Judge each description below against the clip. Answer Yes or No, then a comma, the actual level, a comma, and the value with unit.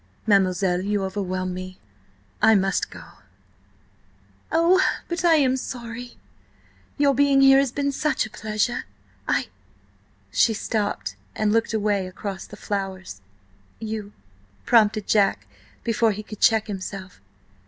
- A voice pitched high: Yes, high, 210 Hz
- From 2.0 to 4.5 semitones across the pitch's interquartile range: Yes, average, 4.2 semitones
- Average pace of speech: No, slow, 115 wpm